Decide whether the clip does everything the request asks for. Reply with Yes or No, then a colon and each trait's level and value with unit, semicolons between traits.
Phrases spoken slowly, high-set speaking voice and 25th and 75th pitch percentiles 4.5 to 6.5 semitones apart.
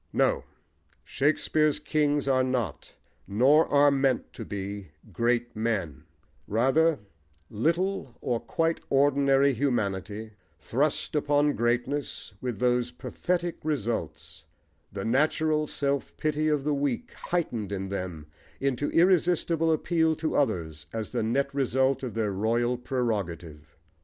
No: slow, 120 wpm; low, 130 Hz; average, 5.2 semitones